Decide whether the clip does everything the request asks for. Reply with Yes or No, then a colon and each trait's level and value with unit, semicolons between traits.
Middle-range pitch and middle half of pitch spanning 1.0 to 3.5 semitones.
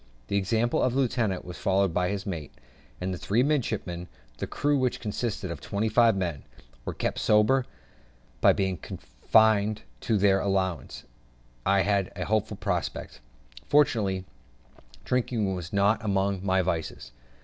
No: low, 100 Hz; average, 3.0 semitones